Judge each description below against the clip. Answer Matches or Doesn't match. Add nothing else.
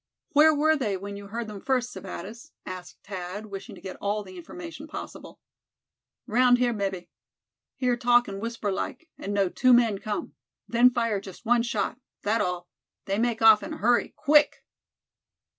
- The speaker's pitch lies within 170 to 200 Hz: Doesn't match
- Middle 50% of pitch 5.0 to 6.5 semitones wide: Doesn't match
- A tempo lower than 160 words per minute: Doesn't match